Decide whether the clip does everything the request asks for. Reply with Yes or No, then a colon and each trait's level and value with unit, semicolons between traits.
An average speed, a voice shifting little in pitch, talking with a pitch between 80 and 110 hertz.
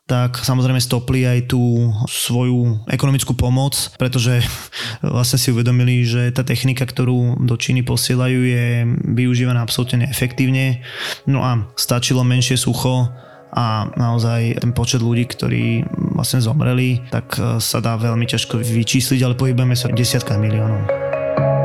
No: average, 135 wpm; narrow, 1.4 semitones; low, 125 Hz